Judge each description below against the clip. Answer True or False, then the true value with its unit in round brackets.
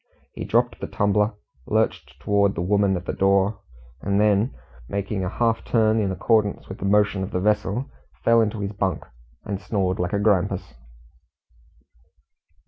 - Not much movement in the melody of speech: True (1.7 semitones)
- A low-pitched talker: True (100 Hz)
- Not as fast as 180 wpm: True (160 wpm)